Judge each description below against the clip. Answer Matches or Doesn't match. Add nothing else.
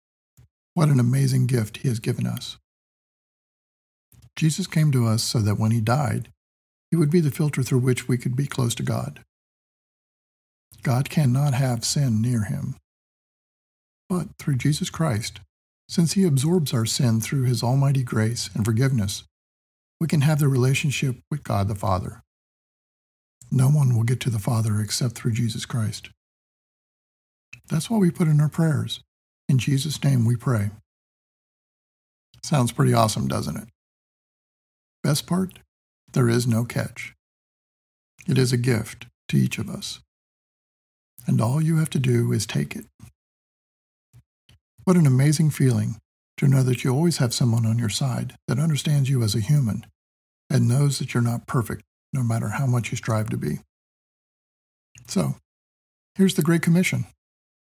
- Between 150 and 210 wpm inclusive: Matches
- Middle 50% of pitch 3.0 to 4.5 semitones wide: Doesn't match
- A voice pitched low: Matches